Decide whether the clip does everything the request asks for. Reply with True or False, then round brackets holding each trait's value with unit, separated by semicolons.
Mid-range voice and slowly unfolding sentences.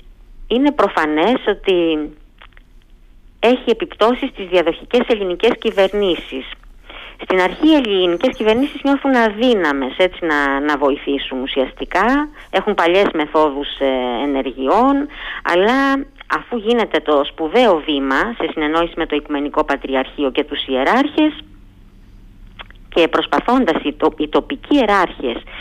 True (170 Hz; 110 wpm)